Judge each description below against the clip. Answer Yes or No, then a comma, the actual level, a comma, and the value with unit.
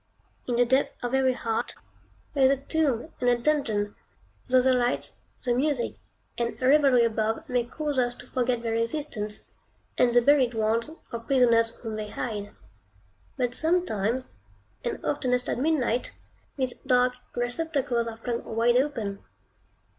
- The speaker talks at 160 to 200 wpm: No, average, 150 wpm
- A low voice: No, high, 245 Hz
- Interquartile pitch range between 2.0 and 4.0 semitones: Yes, narrow, 2.5 semitones